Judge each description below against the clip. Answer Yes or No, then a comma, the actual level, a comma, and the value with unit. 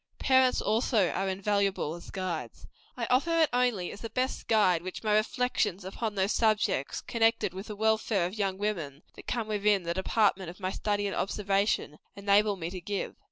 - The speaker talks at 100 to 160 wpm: No, average, 185 wpm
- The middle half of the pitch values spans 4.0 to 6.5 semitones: No, average, 2.8 semitones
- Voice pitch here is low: No, high, 205 Hz